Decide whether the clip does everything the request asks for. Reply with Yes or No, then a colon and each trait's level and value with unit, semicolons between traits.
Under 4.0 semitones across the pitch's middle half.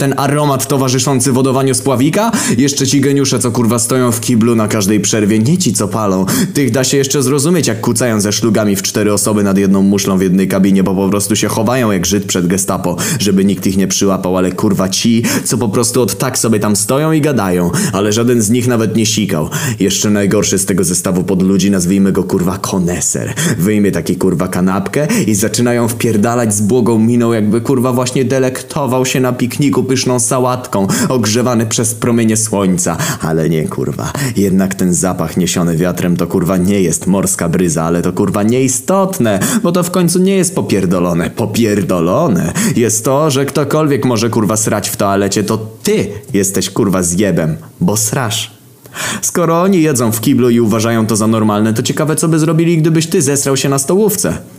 No: average, 5.2 semitones